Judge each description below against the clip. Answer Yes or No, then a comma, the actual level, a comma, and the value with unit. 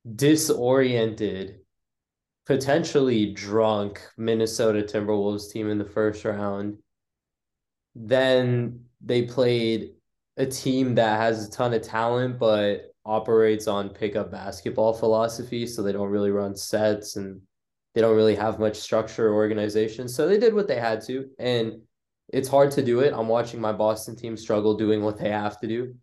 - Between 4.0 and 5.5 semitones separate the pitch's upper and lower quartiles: No, narrow, 2.4 semitones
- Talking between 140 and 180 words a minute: Yes, average, 155 wpm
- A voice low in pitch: Yes, low, 110 Hz